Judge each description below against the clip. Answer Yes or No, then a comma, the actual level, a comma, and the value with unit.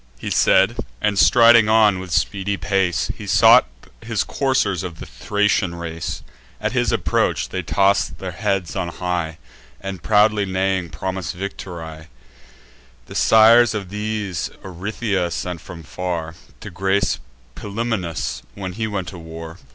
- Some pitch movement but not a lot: Yes, average, 3.2 semitones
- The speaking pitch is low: Yes, very low, 95 Hz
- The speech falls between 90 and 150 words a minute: Yes, average, 140 wpm